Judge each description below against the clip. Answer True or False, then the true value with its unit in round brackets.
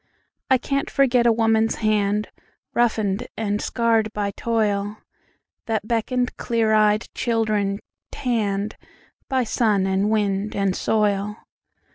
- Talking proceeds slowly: True (100 wpm)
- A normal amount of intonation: False (2.2 semitones)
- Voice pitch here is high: True (215 Hz)